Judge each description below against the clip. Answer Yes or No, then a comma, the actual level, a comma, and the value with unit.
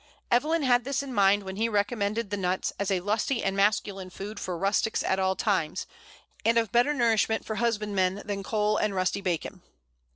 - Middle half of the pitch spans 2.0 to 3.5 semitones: Yes, average, 3.0 semitones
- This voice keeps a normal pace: Yes, average, 190 wpm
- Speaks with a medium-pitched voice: No, high, 205 Hz